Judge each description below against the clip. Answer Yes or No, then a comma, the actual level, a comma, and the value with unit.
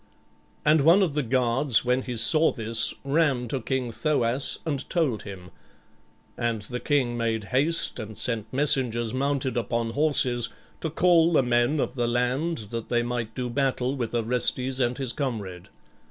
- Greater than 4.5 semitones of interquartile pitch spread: No, average, 3.3 semitones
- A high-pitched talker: No, low, 125 Hz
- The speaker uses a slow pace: No, average, 165 wpm